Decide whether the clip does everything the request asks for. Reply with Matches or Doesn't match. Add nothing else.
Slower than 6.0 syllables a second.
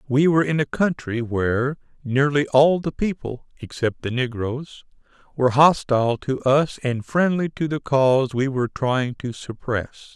Matches